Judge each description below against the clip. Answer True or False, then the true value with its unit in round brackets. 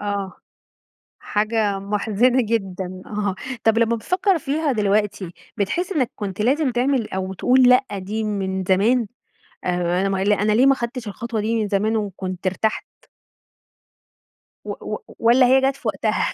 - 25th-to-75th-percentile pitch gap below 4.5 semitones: True (4.1 semitones)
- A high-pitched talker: True (215 Hz)